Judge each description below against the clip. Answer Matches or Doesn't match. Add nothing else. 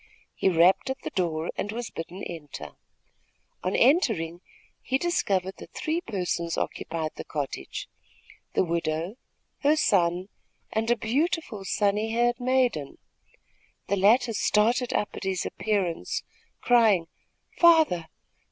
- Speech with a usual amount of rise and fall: Doesn't match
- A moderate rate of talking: Doesn't match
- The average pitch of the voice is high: Matches